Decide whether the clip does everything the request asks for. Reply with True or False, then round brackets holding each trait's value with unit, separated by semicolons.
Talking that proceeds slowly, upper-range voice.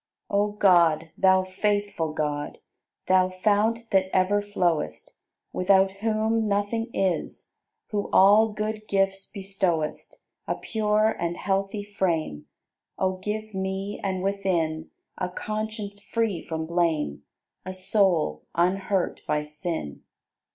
True (115 wpm; 195 Hz)